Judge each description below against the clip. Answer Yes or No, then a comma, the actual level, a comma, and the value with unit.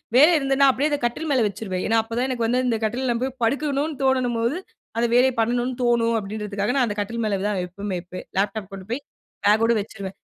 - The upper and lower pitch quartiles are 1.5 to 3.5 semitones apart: No, average, 4.0 semitones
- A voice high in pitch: Yes, high, 235 Hz